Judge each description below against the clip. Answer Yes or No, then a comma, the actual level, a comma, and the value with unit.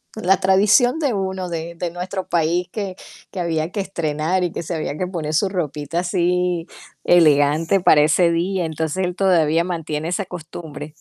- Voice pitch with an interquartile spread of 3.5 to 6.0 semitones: No, average, 2.8 semitones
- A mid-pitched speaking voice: Yes, medium, 175 Hz